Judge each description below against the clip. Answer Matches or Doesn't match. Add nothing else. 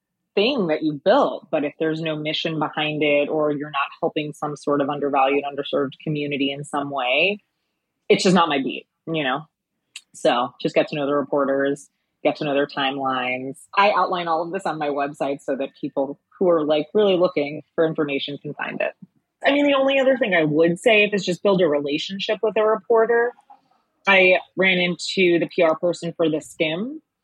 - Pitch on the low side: Doesn't match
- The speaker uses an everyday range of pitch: Matches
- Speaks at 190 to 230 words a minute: Matches